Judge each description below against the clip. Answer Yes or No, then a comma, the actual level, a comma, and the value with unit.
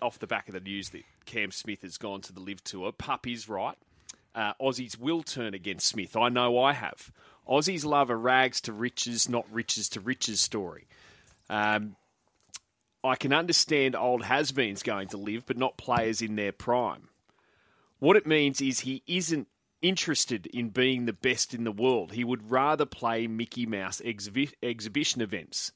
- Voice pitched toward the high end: No, low, 120 Hz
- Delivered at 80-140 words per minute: No, average, 180 wpm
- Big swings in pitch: No, average, 3.5 semitones